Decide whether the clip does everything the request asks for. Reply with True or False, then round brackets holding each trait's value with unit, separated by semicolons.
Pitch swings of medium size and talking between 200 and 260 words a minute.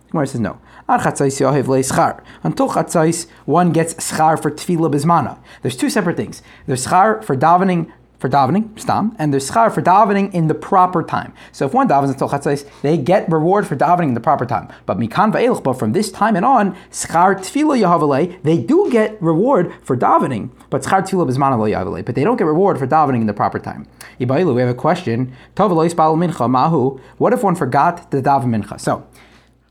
False (4.3 semitones; 165 wpm)